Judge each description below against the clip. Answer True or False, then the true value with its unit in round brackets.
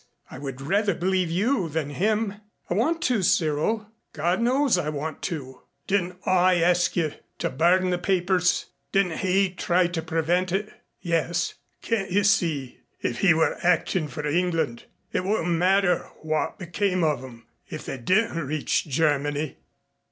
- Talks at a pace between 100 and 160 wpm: True (155 wpm)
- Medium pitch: True (175 Hz)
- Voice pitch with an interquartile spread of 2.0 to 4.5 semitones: True (3.7 semitones)